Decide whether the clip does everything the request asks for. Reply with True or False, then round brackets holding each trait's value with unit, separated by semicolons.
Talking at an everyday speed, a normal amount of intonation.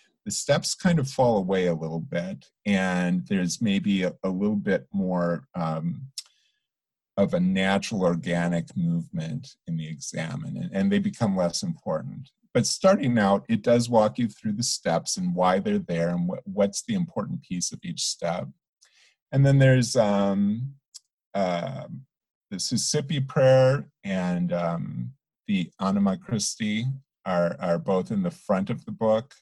False (155 wpm; 8.9 semitones)